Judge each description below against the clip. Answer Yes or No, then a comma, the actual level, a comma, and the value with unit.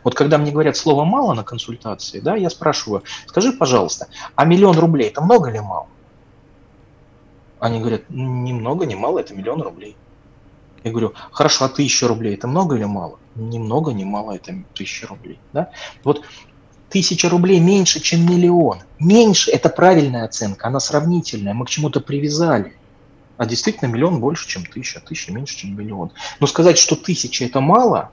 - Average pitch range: No, wide, 6.5 semitones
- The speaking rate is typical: No, fast, 170 wpm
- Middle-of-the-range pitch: Yes, medium, 145 Hz